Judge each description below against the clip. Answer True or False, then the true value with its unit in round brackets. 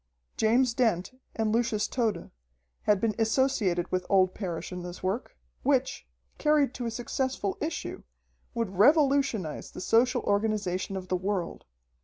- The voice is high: True (215 Hz)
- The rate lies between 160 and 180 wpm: False (140 wpm)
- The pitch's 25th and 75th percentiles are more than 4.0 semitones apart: True (4.8 semitones)